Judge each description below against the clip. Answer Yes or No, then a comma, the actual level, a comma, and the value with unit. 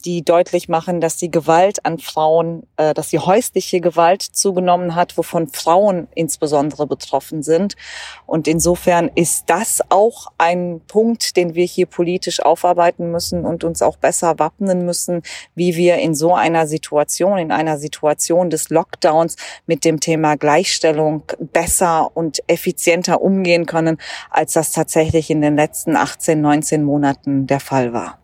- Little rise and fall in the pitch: Yes, narrow, 2.1 semitones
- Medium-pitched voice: Yes, medium, 165 Hz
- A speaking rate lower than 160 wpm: Yes, average, 150 wpm